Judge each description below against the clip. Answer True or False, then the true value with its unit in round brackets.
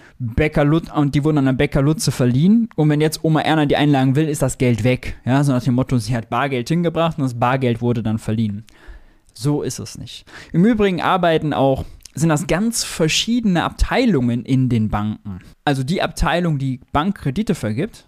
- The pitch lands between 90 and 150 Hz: True (140 Hz)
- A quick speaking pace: True (195 wpm)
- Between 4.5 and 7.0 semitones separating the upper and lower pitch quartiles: True (4.8 semitones)